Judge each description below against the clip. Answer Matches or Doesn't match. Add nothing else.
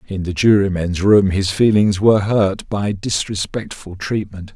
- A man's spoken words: Matches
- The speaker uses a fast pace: Doesn't match